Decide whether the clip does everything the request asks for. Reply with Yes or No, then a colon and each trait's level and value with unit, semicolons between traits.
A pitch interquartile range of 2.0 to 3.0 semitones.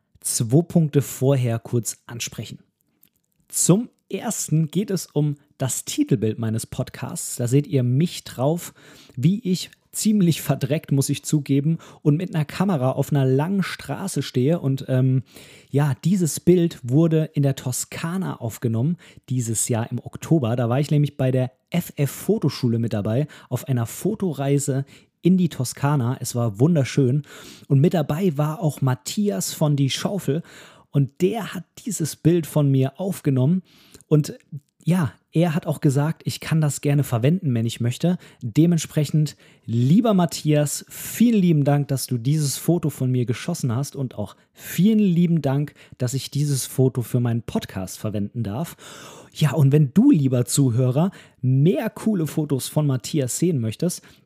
No: average, 4.2 semitones